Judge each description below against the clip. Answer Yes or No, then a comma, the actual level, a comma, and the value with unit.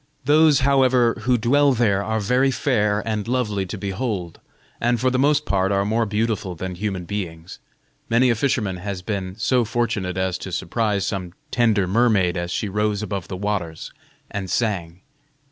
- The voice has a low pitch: Yes, low, 105 Hz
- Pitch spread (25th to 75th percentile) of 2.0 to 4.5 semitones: Yes, average, 4.2 semitones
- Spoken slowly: No, average, 170 wpm